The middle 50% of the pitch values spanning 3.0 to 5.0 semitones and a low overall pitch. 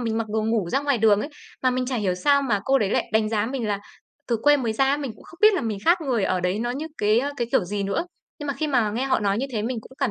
No: average, 4.4 semitones; high, 235 Hz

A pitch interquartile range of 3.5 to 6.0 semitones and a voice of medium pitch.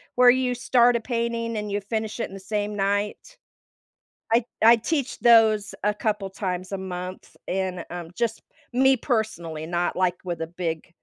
No: average, 4.1 semitones; high, 210 Hz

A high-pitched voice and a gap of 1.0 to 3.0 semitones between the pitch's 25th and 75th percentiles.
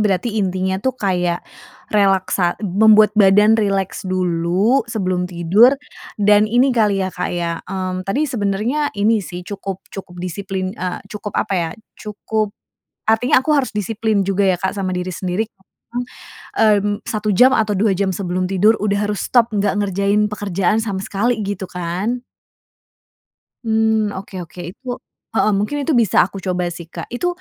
Yes: high, 200 Hz; average, 2.7 semitones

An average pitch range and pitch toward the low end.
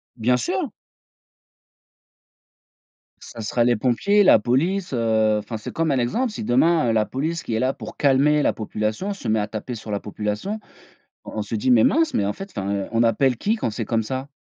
No: wide, 5.7 semitones; low, 120 Hz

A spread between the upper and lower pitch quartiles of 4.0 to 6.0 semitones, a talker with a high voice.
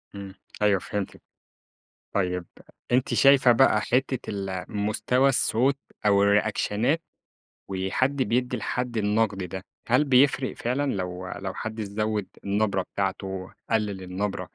No: average, 4.4 semitones; low, 105 Hz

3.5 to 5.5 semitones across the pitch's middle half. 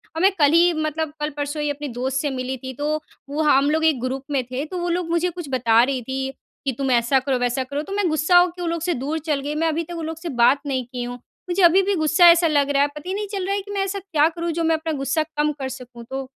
Yes: average, 4.0 semitones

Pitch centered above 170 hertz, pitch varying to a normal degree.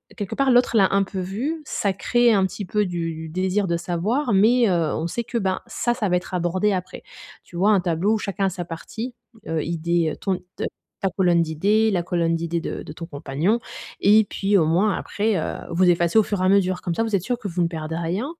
Yes: medium, 185 Hz; average, 3.7 semitones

